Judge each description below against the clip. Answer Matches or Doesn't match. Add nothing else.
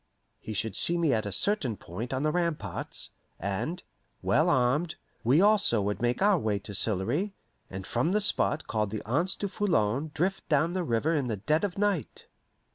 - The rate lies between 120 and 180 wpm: Doesn't match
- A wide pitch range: Matches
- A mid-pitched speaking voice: Matches